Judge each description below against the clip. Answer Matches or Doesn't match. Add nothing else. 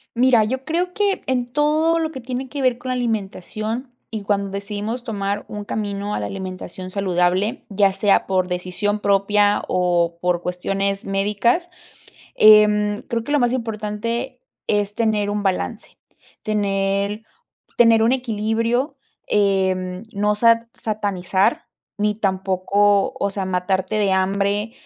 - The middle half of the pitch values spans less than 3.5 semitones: Matches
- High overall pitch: Matches